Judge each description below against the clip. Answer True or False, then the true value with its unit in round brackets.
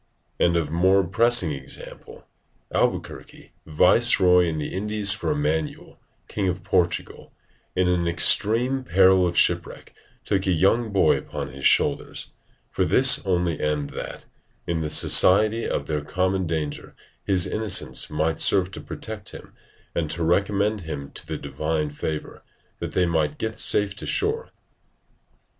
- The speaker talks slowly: False (150 wpm)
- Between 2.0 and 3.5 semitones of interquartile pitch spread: False (4.2 semitones)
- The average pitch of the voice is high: False (90 Hz)